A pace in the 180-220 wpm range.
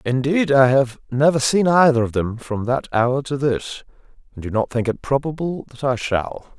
Yes: average, 200 wpm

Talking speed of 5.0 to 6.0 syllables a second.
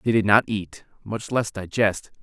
No: 4.4 syllables/s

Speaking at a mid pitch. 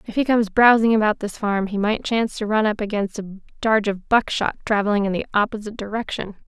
No: high, 215 Hz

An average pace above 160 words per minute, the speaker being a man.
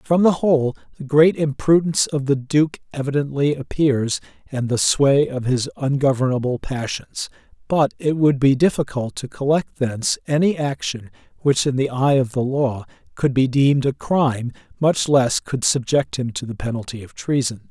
Yes: average, 170 wpm; male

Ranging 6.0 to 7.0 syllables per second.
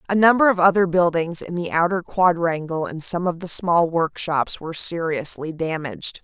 No: 5.0 syllables/s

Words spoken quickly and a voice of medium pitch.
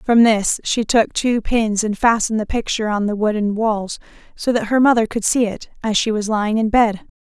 No: fast, 225 wpm; high, 220 Hz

